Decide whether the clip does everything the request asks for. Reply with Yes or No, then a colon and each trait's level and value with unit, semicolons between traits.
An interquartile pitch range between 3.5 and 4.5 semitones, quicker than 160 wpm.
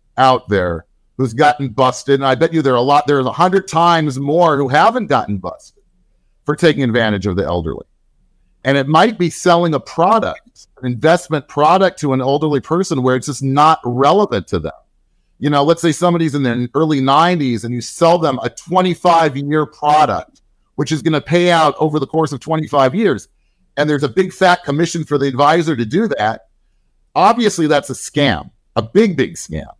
Yes: average, 3.9 semitones; average, 195 wpm